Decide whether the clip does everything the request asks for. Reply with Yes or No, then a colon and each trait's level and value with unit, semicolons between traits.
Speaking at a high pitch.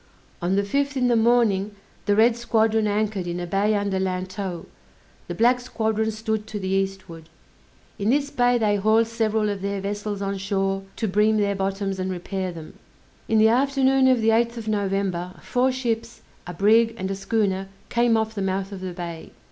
Yes: high, 210 Hz